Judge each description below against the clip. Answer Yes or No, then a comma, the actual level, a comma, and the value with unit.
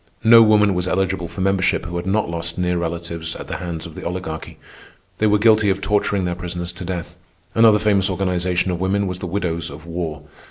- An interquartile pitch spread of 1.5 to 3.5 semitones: Yes, narrow, 2.5 semitones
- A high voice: No, very low, 90 Hz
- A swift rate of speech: Yes, fast, 210 wpm